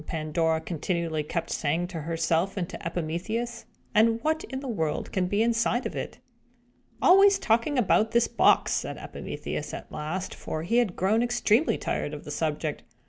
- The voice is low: No, medium, 185 Hz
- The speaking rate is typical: Yes, average, 170 wpm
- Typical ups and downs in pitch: No, wide, 6.4 semitones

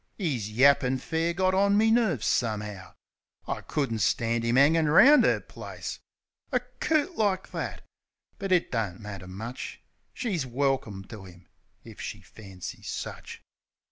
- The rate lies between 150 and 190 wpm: No, average, 140 wpm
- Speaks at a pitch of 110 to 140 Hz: Yes, low, 135 Hz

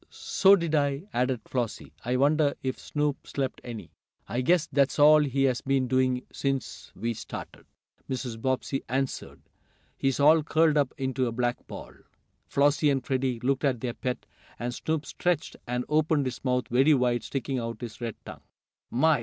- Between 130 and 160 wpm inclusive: No, average, 170 wpm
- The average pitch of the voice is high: No, low, 135 Hz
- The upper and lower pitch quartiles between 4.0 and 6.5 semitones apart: No, average, 2.8 semitones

